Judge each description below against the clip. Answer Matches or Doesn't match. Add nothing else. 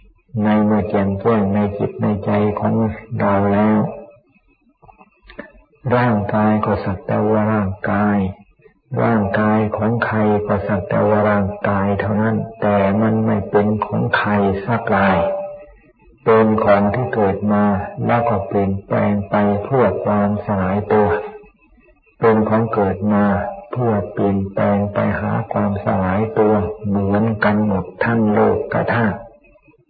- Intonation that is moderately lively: Doesn't match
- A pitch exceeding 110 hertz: Doesn't match